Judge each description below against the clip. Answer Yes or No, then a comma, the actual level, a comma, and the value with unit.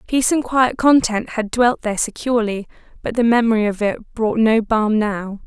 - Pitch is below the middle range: No, high, 225 Hz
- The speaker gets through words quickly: No, average, 185 wpm